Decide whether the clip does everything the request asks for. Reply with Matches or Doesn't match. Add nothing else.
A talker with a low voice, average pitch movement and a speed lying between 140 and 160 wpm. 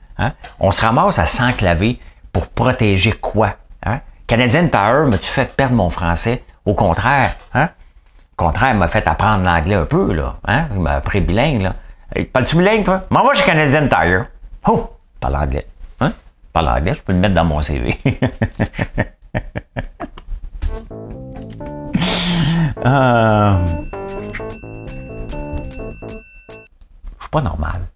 Doesn't match